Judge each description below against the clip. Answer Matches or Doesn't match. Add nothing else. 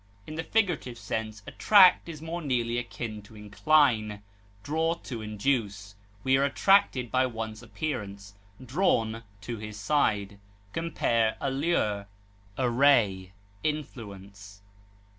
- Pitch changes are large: Matches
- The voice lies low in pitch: Matches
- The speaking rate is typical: Doesn't match